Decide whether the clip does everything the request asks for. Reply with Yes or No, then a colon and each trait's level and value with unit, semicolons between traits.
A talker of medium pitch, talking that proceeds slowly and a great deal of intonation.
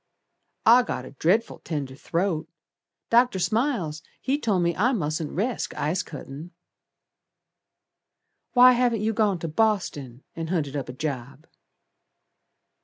Yes: medium, 175 Hz; slow, 125 wpm; wide, 7.2 semitones